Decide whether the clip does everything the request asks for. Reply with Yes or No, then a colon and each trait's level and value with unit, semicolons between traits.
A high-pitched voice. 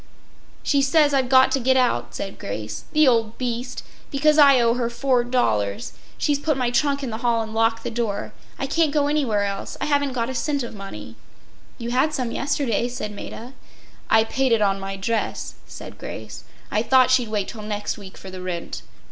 Yes: high, 240 Hz